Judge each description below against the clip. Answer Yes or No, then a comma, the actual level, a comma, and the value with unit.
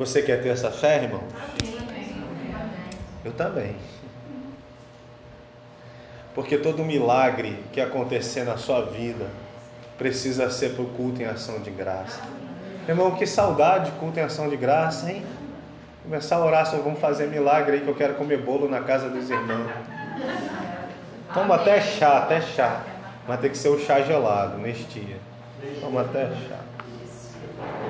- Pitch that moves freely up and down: No, average, 3.8 semitones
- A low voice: Yes, low, 130 Hz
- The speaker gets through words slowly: No, average, 145 wpm